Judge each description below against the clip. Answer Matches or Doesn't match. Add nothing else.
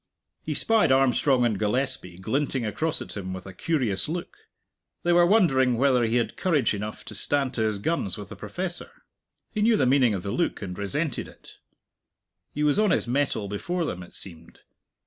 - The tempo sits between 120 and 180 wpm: Doesn't match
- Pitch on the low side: Matches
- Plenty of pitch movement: Matches